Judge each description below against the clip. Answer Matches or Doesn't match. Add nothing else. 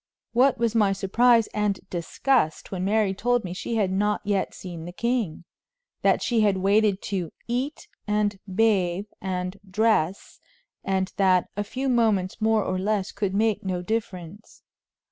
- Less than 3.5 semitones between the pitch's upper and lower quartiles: Matches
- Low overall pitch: Doesn't match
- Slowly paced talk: Doesn't match